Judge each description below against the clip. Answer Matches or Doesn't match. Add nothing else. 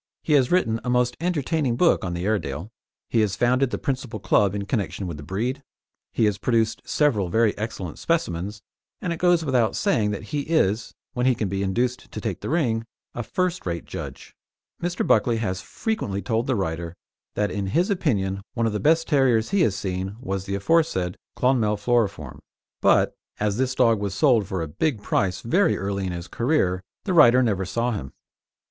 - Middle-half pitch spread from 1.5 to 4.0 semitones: Doesn't match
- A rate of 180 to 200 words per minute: Matches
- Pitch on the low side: Matches